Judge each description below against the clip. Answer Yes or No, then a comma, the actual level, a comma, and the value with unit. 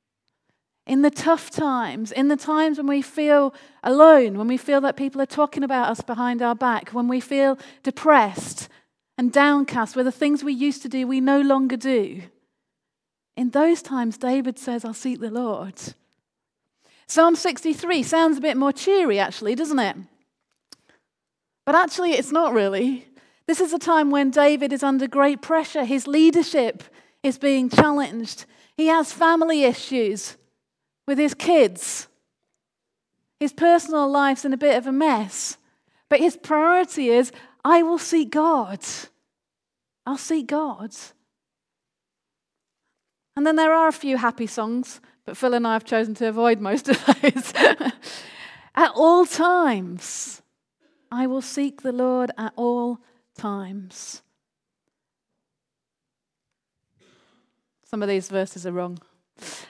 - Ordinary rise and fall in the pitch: Yes, average, 3.9 semitones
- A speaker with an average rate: Yes, average, 145 wpm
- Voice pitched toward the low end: No, very high, 275 Hz